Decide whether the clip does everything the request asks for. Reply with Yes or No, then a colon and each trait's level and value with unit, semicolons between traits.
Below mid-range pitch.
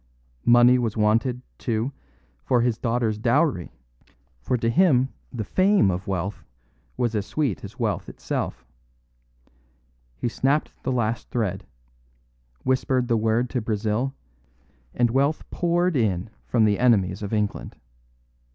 Yes: low, 120 Hz